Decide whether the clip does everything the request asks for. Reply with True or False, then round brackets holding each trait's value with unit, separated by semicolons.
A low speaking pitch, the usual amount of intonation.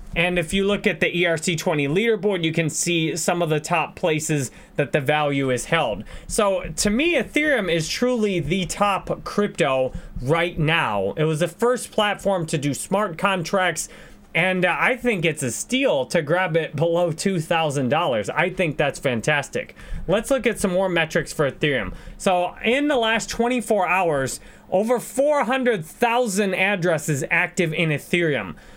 False (180 Hz; 4.1 semitones)